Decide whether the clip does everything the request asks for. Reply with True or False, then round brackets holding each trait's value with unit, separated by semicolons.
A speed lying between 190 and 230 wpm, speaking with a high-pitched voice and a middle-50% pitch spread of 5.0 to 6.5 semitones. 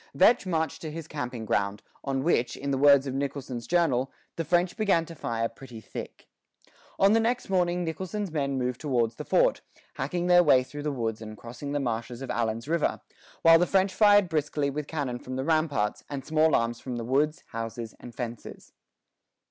False (195 wpm; 140 Hz; 5.4 semitones)